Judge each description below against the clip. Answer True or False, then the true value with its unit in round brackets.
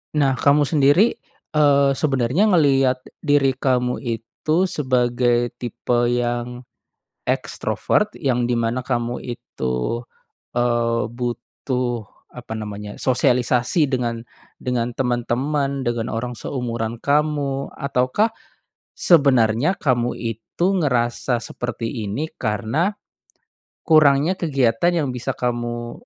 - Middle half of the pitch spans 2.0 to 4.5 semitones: True (3.0 semitones)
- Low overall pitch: True (125 Hz)